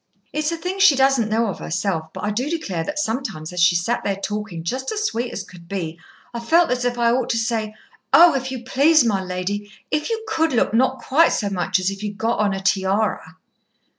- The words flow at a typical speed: No, fast, 230 wpm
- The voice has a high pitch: Yes, high, 225 Hz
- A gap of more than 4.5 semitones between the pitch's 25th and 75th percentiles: Yes, wide, 5.5 semitones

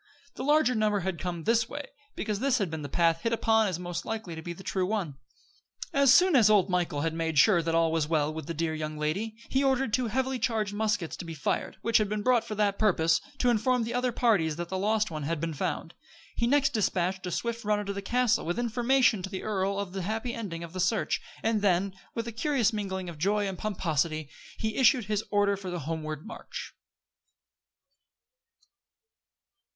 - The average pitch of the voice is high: Yes, high, 200 Hz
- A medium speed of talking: No, fast, 215 wpm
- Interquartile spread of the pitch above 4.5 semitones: Yes, average, 5.1 semitones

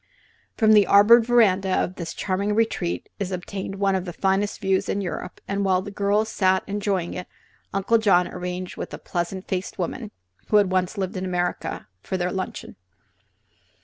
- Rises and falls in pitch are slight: Yes, narrow, 1.8 semitones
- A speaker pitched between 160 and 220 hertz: Yes, high, 190 Hz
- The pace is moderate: Yes, average, 180 wpm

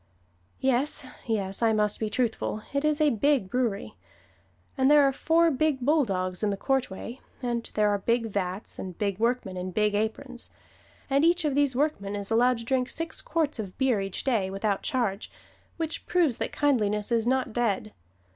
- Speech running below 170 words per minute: No, average, 180 wpm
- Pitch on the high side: Yes, high, 235 Hz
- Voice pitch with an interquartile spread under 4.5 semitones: No, average, 5.2 semitones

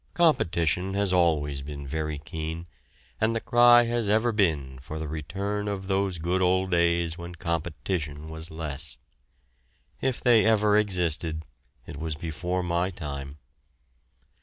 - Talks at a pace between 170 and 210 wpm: No, slow, 135 wpm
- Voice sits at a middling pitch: No, very low, 85 Hz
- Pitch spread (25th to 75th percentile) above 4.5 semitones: No, average, 4.1 semitones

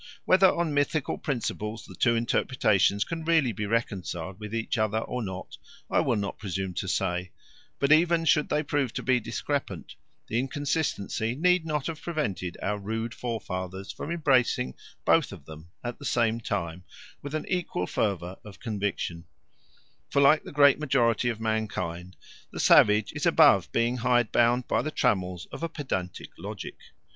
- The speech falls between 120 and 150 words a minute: No, average, 165 wpm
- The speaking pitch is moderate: No, low, 115 Hz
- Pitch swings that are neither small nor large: No, wide, 6.6 semitones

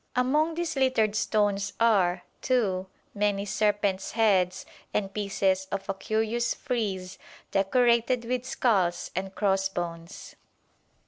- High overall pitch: Yes, high, 205 Hz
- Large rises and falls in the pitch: No, average, 3.5 semitones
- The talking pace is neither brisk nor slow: No, slow, 110 wpm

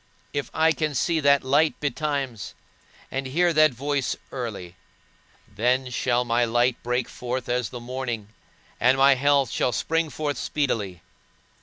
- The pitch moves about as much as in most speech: Yes, average, 3.0 semitones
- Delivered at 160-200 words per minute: No, average, 145 wpm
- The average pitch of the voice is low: Yes, low, 130 Hz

